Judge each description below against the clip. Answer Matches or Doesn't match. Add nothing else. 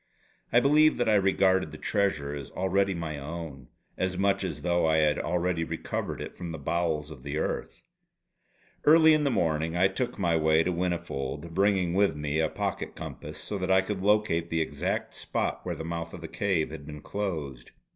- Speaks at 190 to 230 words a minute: Matches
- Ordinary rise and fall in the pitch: Matches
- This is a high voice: Doesn't match